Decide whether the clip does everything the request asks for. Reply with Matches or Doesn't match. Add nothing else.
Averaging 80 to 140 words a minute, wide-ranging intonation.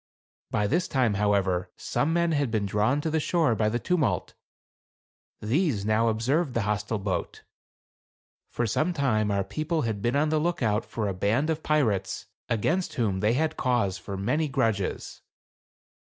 Doesn't match